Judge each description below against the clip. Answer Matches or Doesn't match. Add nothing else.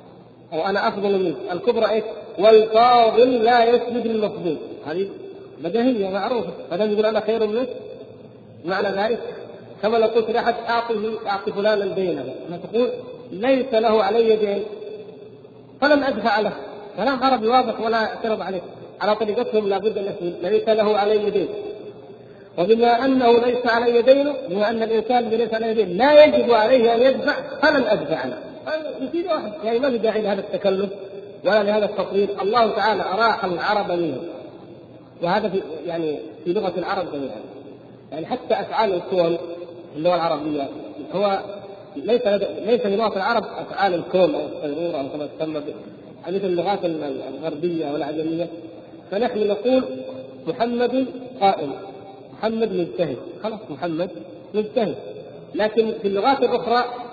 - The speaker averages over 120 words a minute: Matches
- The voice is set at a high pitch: Matches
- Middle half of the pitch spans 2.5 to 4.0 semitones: Doesn't match